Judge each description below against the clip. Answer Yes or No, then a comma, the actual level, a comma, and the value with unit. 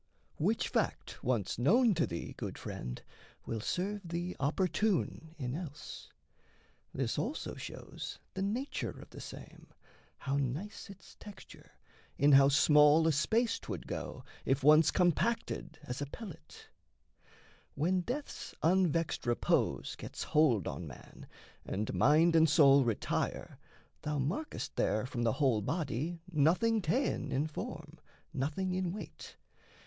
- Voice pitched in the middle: Yes, medium, 155 Hz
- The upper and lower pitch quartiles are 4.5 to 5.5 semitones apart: Yes, average, 5.2 semitones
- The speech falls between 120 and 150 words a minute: Yes, slow, 135 wpm